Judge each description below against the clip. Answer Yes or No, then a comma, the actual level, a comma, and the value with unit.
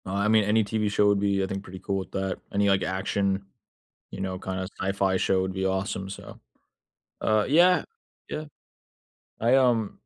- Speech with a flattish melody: Yes, narrow, 2.0 semitones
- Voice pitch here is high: No, low, 100 Hz